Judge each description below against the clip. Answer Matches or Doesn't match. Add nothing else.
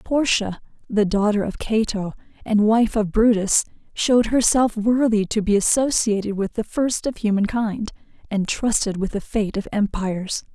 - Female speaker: Matches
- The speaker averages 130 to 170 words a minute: Matches